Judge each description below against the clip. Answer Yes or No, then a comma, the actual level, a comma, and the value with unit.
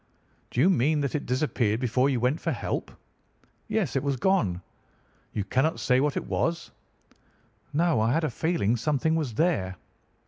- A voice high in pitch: No, medium, 140 Hz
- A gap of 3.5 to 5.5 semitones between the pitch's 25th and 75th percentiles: Yes, average, 5.0 semitones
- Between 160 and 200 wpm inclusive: Yes, average, 175 wpm